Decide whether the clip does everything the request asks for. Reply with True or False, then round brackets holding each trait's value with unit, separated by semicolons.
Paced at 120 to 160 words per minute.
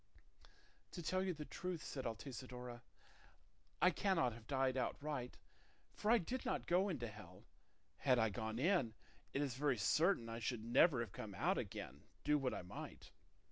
False (170 wpm)